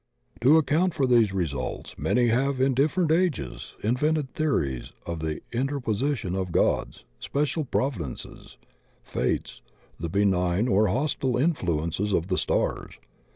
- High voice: No, low, 120 Hz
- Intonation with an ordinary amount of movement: No, wide, 7.8 semitones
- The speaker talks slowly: Yes, slow, 130 wpm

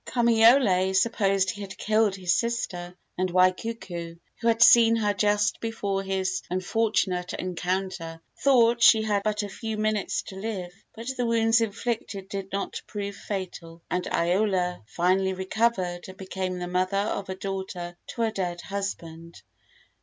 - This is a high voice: Yes, high, 195 Hz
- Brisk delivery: No, average, 155 wpm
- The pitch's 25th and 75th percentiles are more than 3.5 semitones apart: No, average, 3.2 semitones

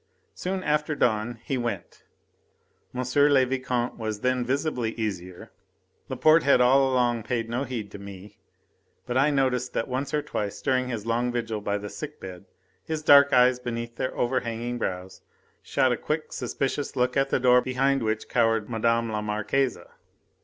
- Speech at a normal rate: Yes, average, 165 wpm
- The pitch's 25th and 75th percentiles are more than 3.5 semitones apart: No, average, 3.1 semitones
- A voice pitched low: Yes, low, 125 Hz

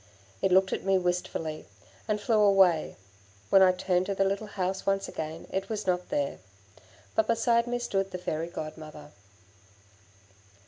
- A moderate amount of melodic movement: No, narrow, 2.3 semitones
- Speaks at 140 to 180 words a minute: Yes, average, 155 wpm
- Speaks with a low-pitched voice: No, high, 190 Hz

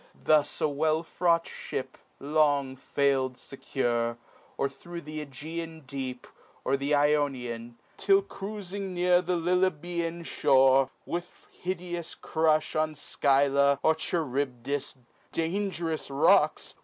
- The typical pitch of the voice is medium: Yes, medium, 155 Hz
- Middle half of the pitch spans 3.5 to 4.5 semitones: Yes, average, 3.9 semitones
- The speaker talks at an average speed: No, slow, 110 wpm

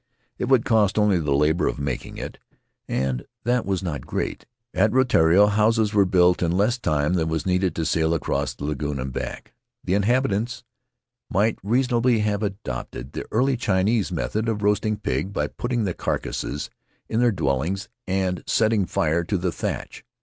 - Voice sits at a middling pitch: No, very low, 95 Hz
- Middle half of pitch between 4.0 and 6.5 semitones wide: Yes, average, 5.3 semitones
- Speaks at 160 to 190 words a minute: Yes, average, 175 wpm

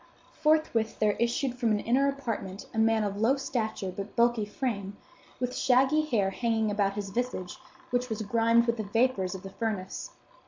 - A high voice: Yes, high, 225 Hz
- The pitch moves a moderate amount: Yes, average, 3.4 semitones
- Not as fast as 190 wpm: Yes, average, 180 wpm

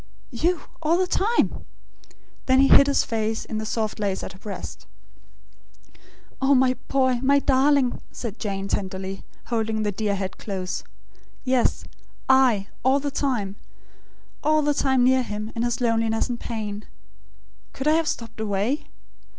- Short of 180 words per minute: Yes, average, 150 wpm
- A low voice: No, high, 235 Hz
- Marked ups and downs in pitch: No, average, 4.3 semitones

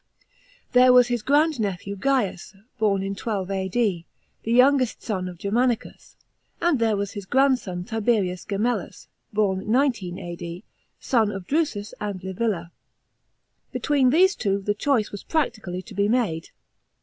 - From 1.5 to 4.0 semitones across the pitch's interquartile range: No, average, 4.7 semitones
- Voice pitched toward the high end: Yes, high, 210 Hz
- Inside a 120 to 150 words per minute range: Yes, average, 145 wpm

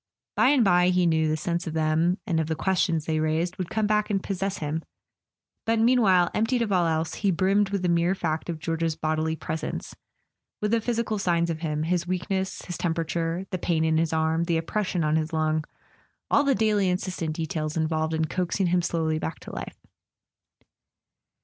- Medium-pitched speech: Yes, medium, 170 Hz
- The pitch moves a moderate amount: Yes, average, 3.2 semitones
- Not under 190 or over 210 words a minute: Yes, average, 195 wpm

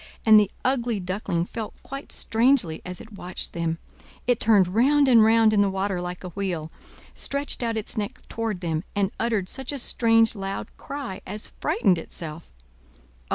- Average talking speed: Yes, average, 170 wpm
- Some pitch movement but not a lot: Yes, average, 4.2 semitones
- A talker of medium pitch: No, high, 210 Hz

